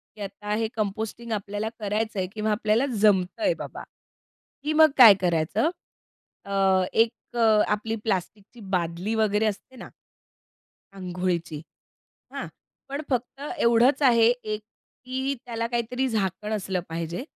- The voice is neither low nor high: No, high, 215 Hz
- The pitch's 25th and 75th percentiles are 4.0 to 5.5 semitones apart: No, average, 3.4 semitones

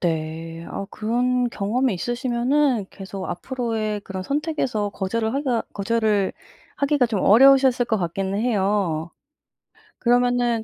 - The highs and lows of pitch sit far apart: No, average, 4.2 semitones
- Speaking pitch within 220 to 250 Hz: Yes, high, 225 Hz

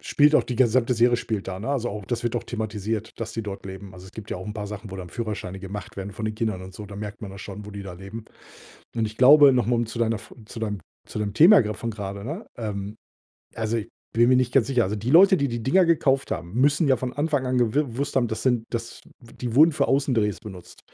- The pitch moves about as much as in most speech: Yes, average, 3.8 semitones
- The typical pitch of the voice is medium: No, low, 115 Hz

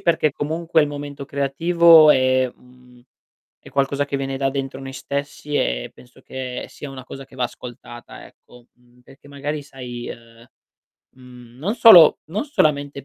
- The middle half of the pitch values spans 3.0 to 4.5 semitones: No, narrow, 2.6 semitones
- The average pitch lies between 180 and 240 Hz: No, low, 135 Hz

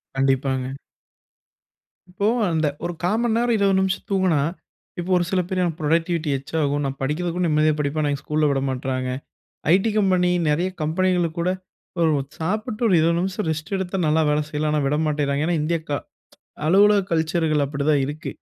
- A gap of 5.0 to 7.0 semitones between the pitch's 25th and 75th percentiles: No, average, 3.8 semitones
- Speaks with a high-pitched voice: No, medium, 160 Hz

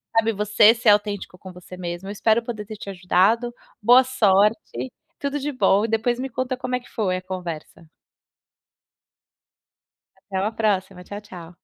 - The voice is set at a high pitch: Yes, high, 210 Hz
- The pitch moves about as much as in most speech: Yes, average, 3.8 semitones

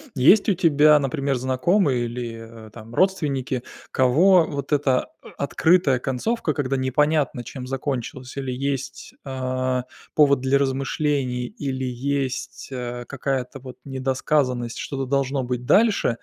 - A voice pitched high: No, low, 135 Hz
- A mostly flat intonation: Yes, narrow, 2.2 semitones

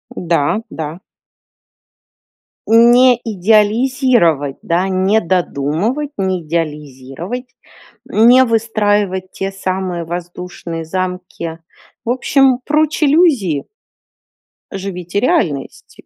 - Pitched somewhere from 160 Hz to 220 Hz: Yes, high, 190 Hz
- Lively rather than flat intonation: Yes, wide, 5.7 semitones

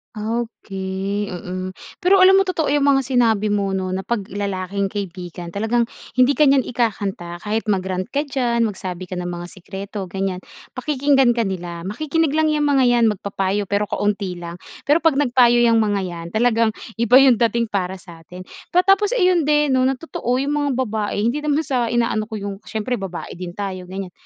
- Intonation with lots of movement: Yes, wide, 5.7 semitones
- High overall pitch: Yes, high, 220 Hz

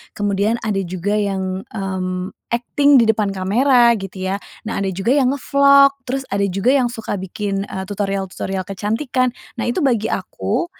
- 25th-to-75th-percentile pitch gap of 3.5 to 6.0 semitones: Yes, average, 4.2 semitones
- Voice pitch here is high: Yes, high, 205 Hz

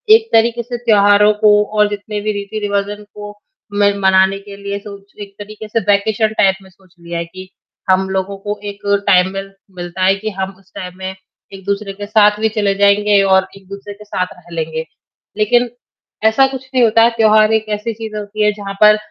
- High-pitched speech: Yes, high, 205 Hz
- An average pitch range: No, narrow, 1.9 semitones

